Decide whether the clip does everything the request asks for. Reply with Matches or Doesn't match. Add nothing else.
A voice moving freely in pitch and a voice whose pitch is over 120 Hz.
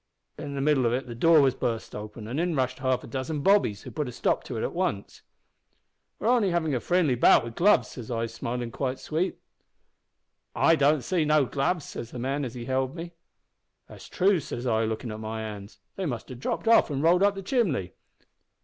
Matches